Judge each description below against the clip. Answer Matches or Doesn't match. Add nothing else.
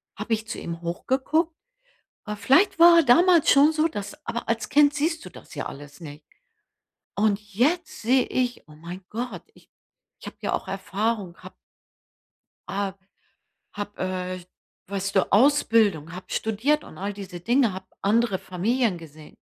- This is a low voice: Doesn't match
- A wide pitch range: Matches